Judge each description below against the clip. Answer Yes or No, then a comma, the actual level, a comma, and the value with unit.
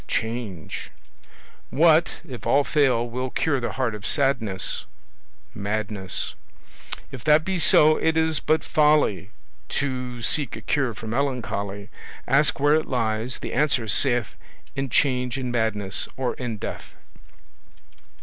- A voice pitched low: Yes, low, 125 Hz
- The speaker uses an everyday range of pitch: Yes, average, 4.5 semitones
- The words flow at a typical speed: No, slow, 130 wpm